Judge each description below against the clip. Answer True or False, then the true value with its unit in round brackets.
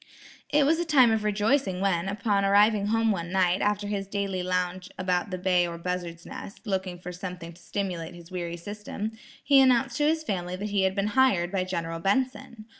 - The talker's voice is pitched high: True (195 Hz)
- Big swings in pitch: False (3.0 semitones)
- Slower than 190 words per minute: False (200 wpm)